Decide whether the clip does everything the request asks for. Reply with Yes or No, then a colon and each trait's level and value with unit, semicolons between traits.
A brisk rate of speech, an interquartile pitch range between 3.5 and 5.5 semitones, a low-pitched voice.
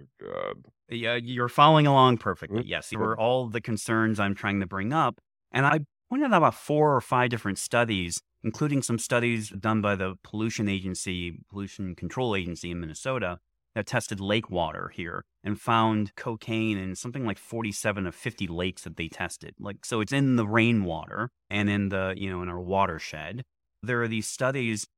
No: average, 185 wpm; average, 4.2 semitones; low, 105 Hz